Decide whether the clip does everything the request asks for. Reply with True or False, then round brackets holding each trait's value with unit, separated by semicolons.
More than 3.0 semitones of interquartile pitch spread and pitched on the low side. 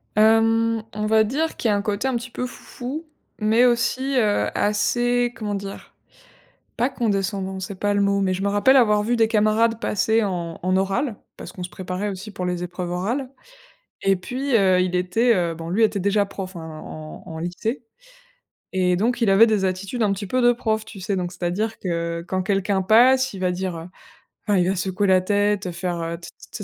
False (3.5 semitones; 205 Hz)